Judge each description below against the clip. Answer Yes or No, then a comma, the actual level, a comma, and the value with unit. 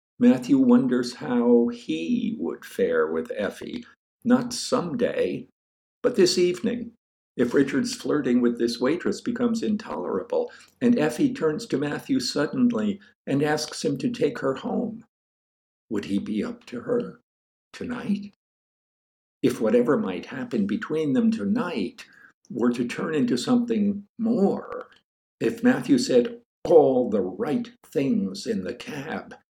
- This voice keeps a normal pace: No, slow, 130 wpm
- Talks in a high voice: Yes, high, 235 Hz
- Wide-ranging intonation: No, average, 3.3 semitones